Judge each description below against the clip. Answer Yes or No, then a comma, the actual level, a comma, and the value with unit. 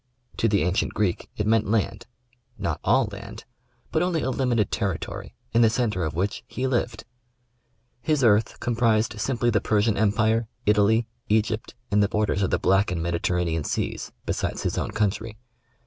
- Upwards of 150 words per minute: Yes, average, 180 wpm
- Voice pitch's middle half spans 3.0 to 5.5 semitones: No, narrow, 2.6 semitones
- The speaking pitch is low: Yes, low, 110 Hz